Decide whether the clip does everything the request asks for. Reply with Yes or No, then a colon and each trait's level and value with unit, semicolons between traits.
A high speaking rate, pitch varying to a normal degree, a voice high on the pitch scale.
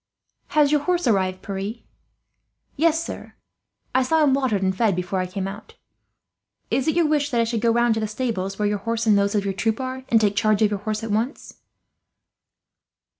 Yes: fast, 210 wpm; average, 4.5 semitones; high, 220 Hz